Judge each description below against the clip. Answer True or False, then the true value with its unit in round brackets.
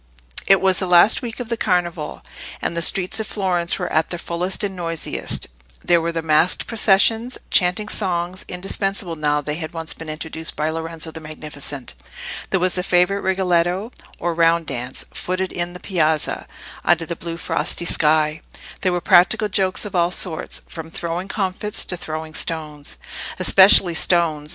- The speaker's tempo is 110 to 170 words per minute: True (165 wpm)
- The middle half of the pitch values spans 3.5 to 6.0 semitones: False (2.7 semitones)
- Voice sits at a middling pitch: True (175 Hz)